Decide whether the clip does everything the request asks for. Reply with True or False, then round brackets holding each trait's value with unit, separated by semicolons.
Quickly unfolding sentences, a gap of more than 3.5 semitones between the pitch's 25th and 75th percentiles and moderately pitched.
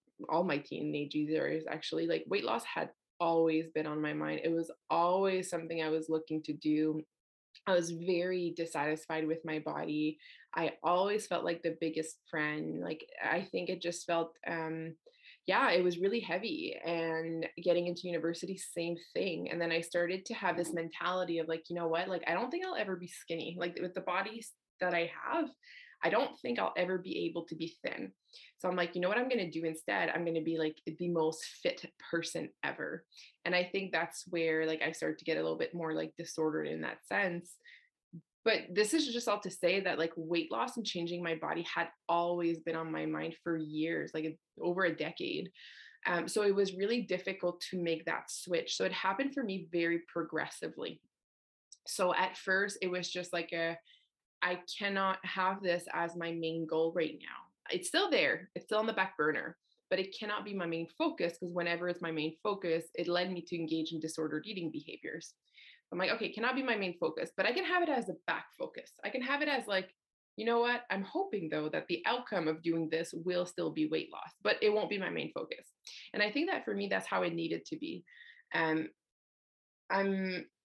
False (215 wpm; 2.7 semitones; 175 Hz)